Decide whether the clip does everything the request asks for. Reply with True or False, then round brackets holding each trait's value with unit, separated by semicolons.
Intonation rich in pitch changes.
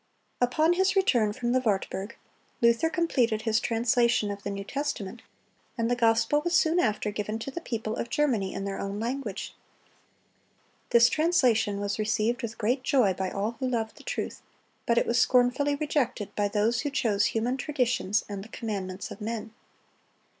False (3.8 semitones)